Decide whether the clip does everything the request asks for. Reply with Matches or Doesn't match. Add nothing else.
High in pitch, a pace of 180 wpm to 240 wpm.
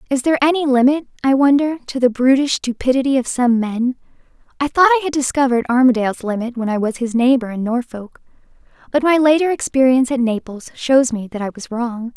Matches